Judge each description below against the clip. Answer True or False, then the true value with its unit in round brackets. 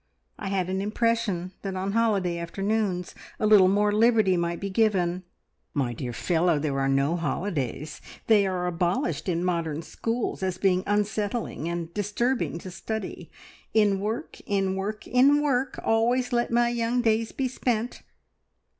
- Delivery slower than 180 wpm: True (155 wpm)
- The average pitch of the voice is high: True (195 Hz)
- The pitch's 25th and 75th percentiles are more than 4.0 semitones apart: True (4.4 semitones)